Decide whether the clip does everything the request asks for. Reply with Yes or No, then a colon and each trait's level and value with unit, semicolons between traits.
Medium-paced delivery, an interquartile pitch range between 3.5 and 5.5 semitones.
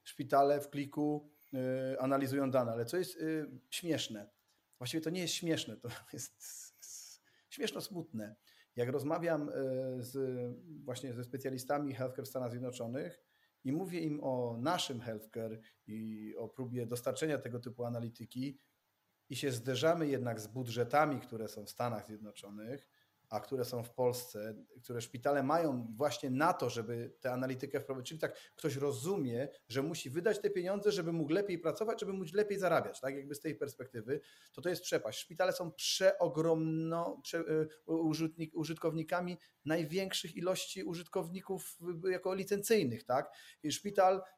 Yes: average, 150 wpm; average, 5.2 semitones